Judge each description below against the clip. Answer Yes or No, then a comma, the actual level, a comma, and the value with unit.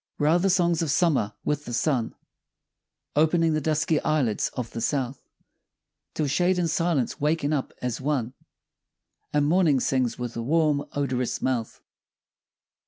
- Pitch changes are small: No, average, 4.1 semitones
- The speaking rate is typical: Yes, average, 150 wpm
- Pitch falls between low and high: Yes, medium, 145 Hz